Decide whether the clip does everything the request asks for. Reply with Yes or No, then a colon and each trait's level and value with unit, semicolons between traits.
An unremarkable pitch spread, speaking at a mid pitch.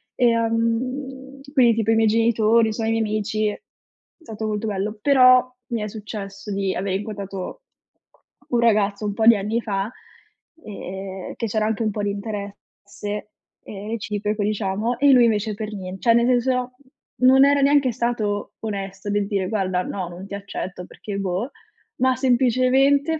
No: average, 3.0 semitones; high, 215 Hz